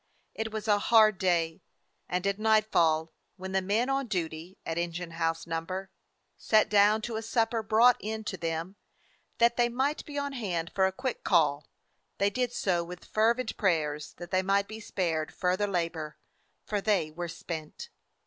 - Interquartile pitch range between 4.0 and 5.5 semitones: Yes, average, 4.7 semitones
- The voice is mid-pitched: No, high, 195 Hz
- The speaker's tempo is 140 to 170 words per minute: No, average, 180 wpm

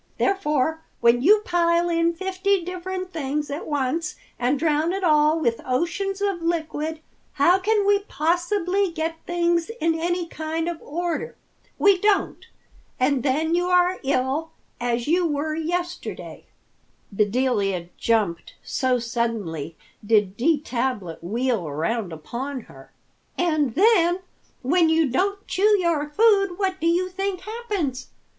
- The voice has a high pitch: Yes, very high, 325 Hz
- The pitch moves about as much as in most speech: No, wide, 5.8 semitones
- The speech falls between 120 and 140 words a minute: Yes, slow, 135 wpm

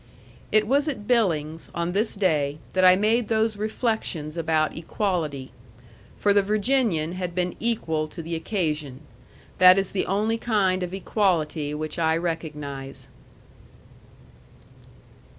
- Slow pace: Yes, slow, 130 wpm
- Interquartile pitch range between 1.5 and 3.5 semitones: No, average, 5.2 semitones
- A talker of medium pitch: Yes, medium, 180 Hz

